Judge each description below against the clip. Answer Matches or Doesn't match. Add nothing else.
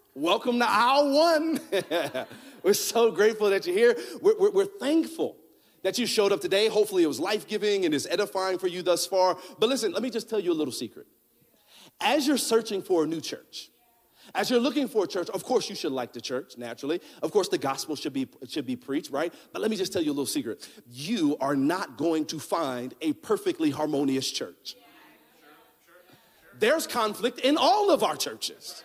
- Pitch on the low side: Doesn't match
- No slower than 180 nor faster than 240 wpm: Matches